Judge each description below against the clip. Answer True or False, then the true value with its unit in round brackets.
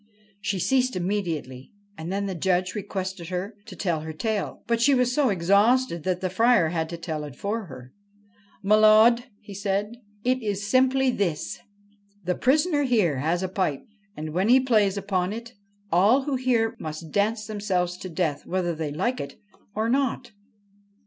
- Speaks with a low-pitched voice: False (200 Hz)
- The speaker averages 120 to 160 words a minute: False (175 wpm)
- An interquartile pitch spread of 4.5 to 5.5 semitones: True (5.1 semitones)